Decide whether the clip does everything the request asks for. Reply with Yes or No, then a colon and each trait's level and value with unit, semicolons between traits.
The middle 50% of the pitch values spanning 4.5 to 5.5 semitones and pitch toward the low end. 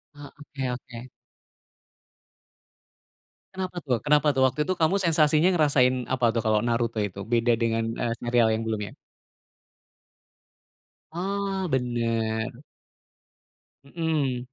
Yes: average, 4.8 semitones; low, 125 Hz